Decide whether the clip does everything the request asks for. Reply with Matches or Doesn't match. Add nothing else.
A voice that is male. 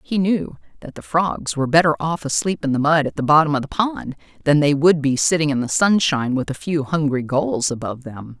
Doesn't match